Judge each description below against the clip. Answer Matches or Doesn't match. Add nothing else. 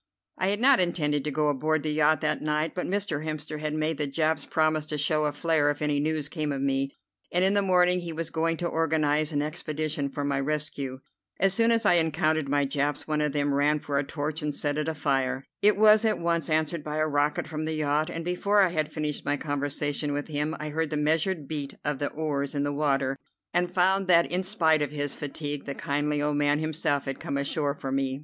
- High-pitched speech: Doesn't match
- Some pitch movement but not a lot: Doesn't match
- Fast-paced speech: Matches